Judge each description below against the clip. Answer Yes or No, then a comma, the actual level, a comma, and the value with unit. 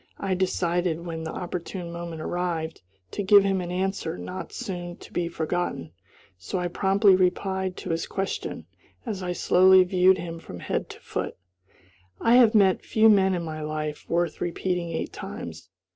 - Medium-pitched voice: Yes, medium, 180 Hz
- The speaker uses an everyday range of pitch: No, narrow, 2.1 semitones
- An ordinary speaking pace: Yes, average, 170 wpm